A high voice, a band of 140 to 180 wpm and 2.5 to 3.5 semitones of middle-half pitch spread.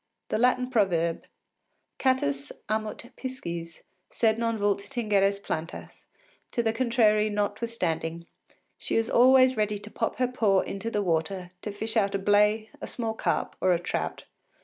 Yes: high, 210 Hz; average, 150 wpm; average, 3.1 semitones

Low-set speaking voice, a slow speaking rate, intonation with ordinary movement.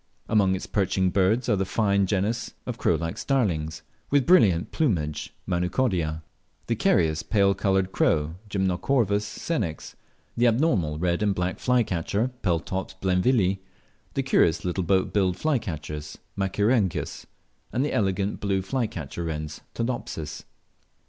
Yes: very low, 95 Hz; slow, 130 wpm; average, 4.3 semitones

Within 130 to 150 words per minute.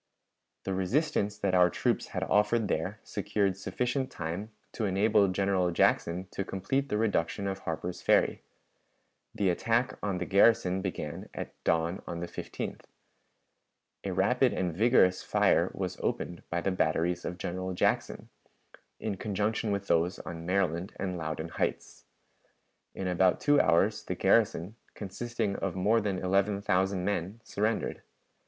Yes: average, 145 wpm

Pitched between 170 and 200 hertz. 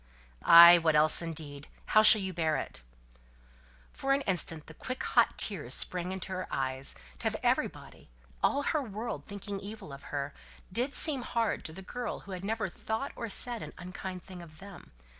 Yes: high, 190 Hz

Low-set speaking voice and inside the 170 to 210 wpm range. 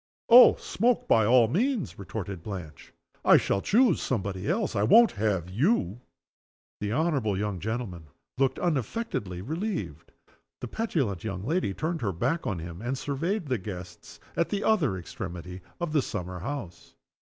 No: low, 115 Hz; average, 155 wpm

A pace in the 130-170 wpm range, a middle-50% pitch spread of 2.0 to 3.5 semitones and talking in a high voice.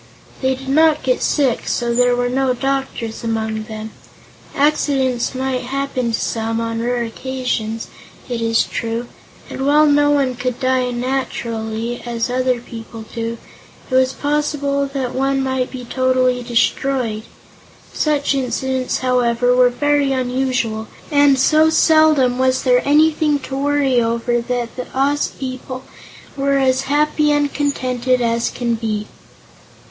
Yes: average, 140 wpm; narrow, 2.5 semitones; very high, 255 Hz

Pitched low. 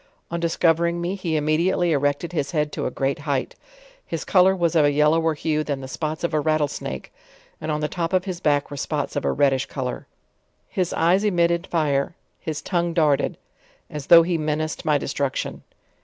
No: medium, 155 Hz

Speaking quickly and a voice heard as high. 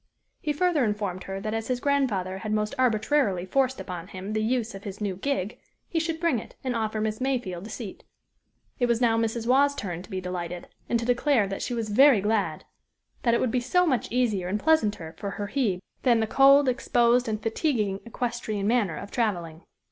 Yes: fast, 210 wpm; high, 225 Hz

